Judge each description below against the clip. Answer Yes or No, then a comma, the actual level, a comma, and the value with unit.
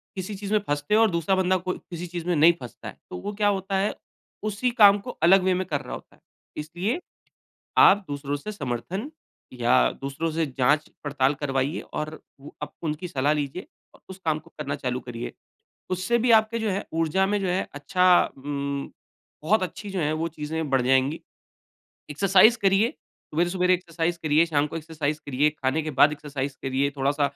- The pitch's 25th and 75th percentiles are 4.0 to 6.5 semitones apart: Yes, average, 5.0 semitones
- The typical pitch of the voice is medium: Yes, medium, 160 Hz